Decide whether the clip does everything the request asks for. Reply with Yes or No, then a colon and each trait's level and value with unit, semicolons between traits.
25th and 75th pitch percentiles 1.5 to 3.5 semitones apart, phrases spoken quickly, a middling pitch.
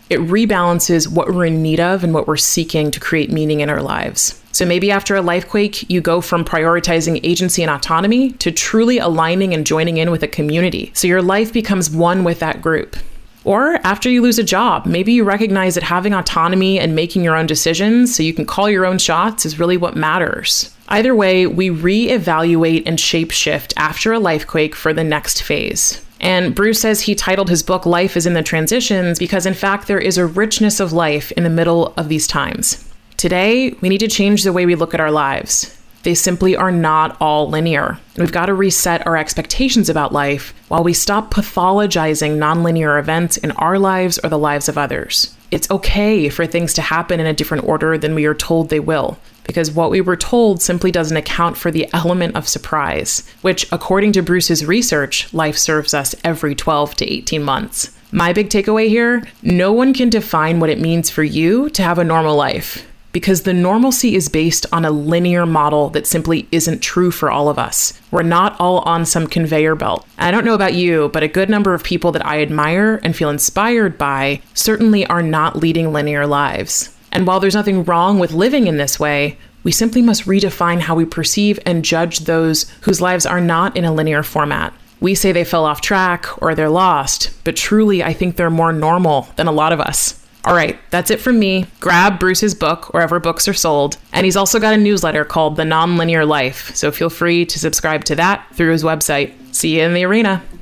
Yes: average, 3.2 semitones; fast, 210 wpm; medium, 170 Hz